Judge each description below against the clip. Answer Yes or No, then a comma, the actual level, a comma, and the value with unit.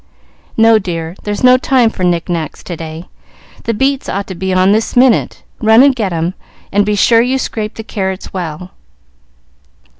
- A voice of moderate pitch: No, high, 205 Hz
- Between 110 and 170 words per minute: No, average, 180 wpm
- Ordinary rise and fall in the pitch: Yes, average, 4.3 semitones